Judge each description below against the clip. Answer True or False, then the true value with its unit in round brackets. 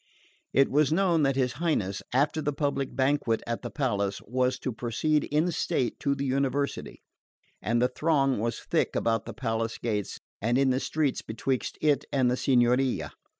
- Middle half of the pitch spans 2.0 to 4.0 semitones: True (3.3 semitones)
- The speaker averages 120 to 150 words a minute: False (175 wpm)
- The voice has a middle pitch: False (130 Hz)